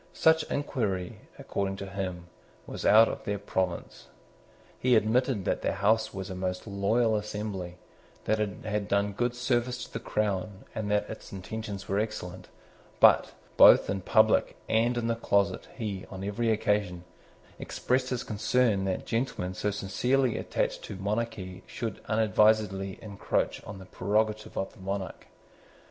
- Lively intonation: No, narrow, 2.6 semitones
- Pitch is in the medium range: No, low, 105 Hz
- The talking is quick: No, average, 155 wpm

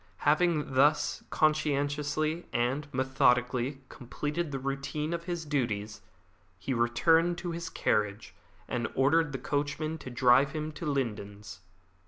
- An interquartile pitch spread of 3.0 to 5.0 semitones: Yes, average, 3.9 semitones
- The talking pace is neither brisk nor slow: No, slow, 130 wpm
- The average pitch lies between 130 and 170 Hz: Yes, medium, 140 Hz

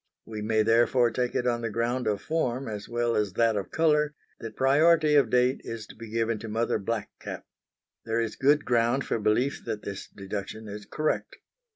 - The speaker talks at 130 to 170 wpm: No, average, 200 wpm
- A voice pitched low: Yes, low, 115 Hz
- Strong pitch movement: No, average, 2.9 semitones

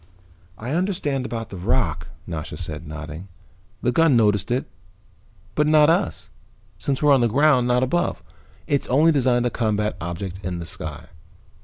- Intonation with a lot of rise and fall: Yes, wide, 7.5 semitones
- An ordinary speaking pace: Yes, average, 160 wpm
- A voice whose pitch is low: Yes, low, 120 Hz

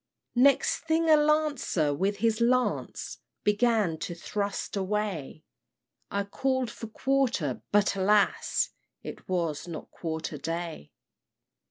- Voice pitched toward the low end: No, high, 205 Hz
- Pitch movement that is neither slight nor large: No, wide, 6.5 semitones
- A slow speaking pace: Yes, slow, 115 wpm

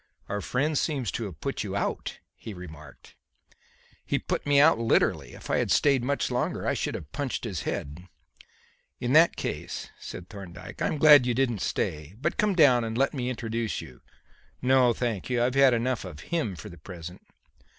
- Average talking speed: Yes, average, 190 wpm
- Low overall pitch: Yes, low, 120 Hz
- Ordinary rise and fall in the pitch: No, wide, 6.6 semitones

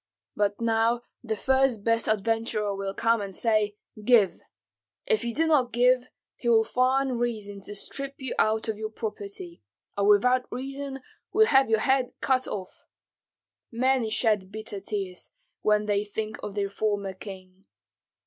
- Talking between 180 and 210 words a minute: No, average, 150 wpm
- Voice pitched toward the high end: Yes, high, 220 Hz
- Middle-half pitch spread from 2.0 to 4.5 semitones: Yes, average, 3.5 semitones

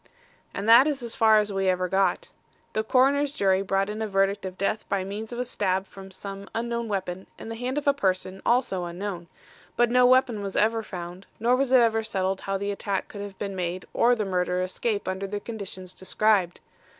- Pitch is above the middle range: Yes, high, 200 Hz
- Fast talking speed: Yes, fast, 215 wpm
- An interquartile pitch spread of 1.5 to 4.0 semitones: Yes, average, 3.3 semitones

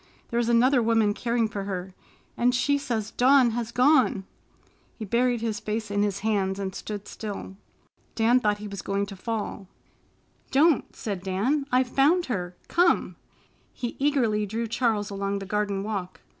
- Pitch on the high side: Yes, high, 220 Hz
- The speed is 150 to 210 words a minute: Yes, average, 165 wpm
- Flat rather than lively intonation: No, average, 3.6 semitones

